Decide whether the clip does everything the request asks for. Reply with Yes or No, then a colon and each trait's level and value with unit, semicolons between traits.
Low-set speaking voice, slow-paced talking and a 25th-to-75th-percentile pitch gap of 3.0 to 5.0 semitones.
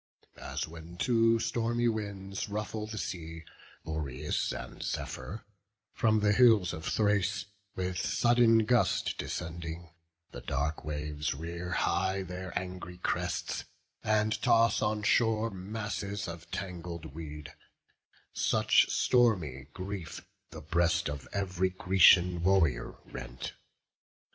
Yes: very low, 95 Hz; slow, 115 wpm; average, 4.4 semitones